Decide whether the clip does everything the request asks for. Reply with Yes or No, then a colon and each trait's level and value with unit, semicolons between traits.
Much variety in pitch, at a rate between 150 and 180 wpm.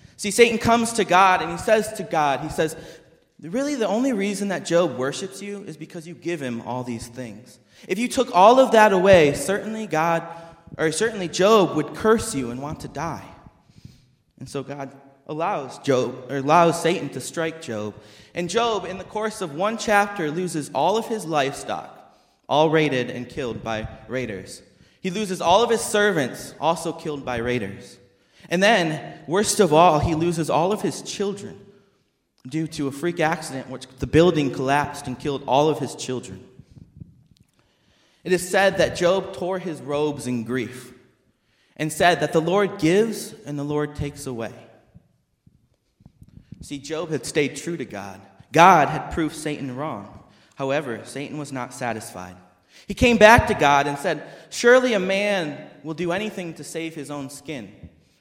Yes: wide, 6.0 semitones; average, 175 wpm